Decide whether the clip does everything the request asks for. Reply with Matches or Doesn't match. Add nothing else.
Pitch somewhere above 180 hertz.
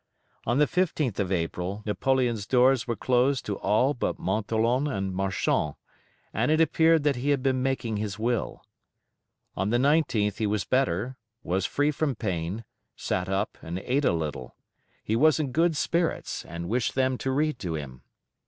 Doesn't match